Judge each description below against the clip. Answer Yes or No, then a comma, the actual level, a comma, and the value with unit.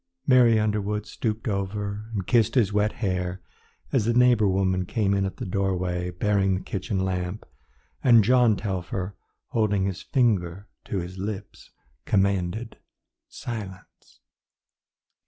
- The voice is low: Yes, low, 100 Hz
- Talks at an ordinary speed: No, slow, 130 wpm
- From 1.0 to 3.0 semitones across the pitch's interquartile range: Yes, average, 2.7 semitones